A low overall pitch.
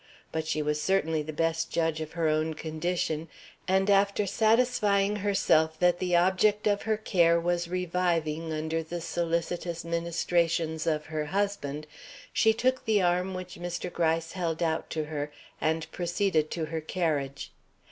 No: medium, 170 Hz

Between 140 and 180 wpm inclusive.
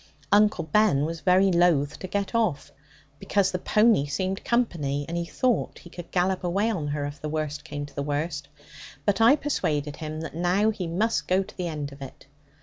No: fast, 205 wpm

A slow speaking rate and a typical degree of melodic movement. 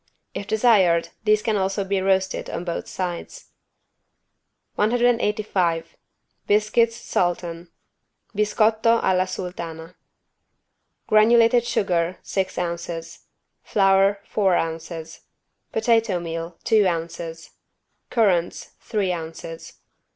Yes: slow, 90 wpm; average, 4.0 semitones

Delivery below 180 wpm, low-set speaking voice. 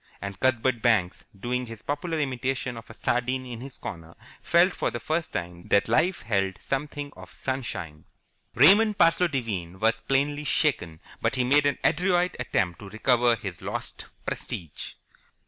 Yes: average, 160 wpm; low, 125 Hz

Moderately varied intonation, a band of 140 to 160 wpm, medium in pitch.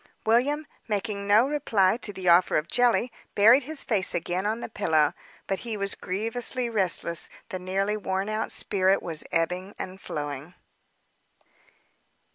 No: average, 3.7 semitones; average, 145 wpm; high, 200 Hz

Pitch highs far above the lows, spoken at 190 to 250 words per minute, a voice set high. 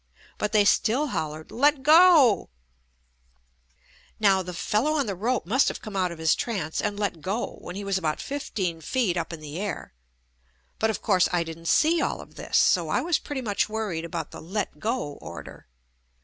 Yes: wide, 6.3 semitones; average, 195 wpm; high, 200 Hz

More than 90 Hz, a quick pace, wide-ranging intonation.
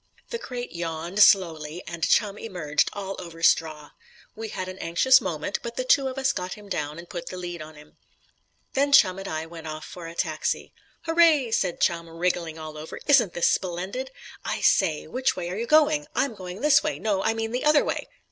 Yes: medium, 185 Hz; fast, 210 wpm; wide, 6.9 semitones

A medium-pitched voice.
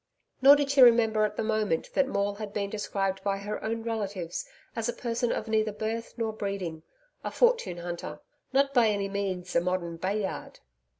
No: high, 210 Hz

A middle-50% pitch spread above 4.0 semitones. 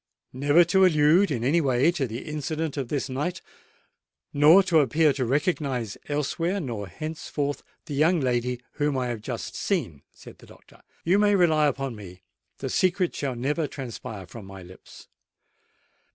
Yes: average, 4.7 semitones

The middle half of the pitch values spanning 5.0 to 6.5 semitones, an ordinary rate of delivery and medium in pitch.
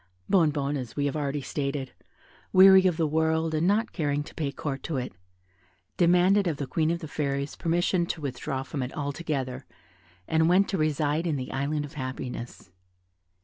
No: average, 3.3 semitones; average, 180 wpm; medium, 150 Hz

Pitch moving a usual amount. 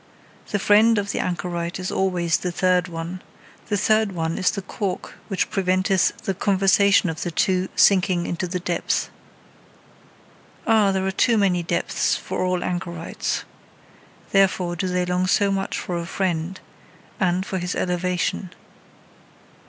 No: narrow, 1.8 semitones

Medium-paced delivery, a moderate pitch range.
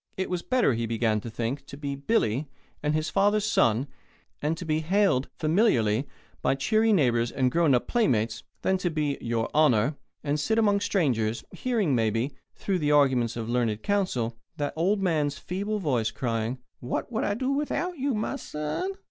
No: average, 180 wpm; wide, 8.8 semitones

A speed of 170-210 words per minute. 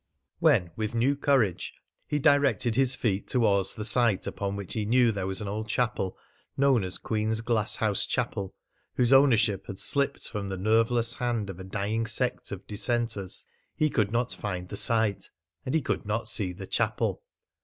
Yes: average, 175 wpm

